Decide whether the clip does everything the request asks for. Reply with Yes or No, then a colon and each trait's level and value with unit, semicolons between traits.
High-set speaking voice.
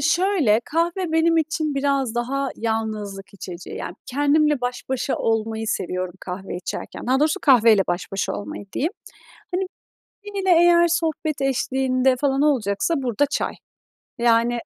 Yes: very high, 265 Hz